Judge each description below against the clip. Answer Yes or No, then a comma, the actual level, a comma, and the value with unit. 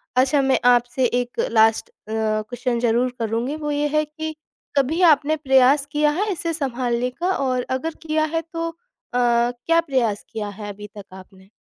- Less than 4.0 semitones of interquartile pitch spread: No, average, 4.4 semitones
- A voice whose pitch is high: Yes, very high, 255 Hz